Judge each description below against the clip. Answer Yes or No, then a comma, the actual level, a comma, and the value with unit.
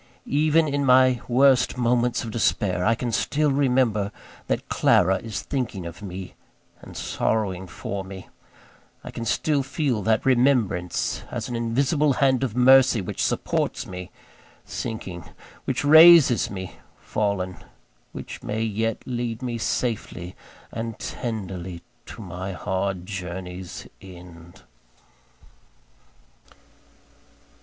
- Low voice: Yes, low, 110 Hz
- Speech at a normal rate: No, slow, 115 wpm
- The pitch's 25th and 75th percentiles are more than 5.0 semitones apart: Yes, wide, 5.4 semitones